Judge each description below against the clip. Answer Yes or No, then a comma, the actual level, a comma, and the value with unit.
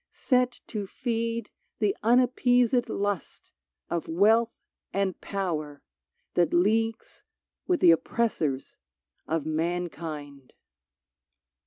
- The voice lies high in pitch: Yes, high, 200 Hz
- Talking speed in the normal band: No, slow, 85 wpm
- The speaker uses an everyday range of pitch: No, wide, 6.0 semitones